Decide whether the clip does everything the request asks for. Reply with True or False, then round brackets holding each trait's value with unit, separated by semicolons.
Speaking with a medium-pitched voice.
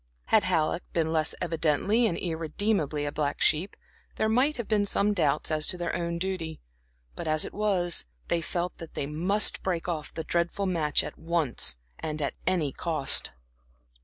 True (170 Hz)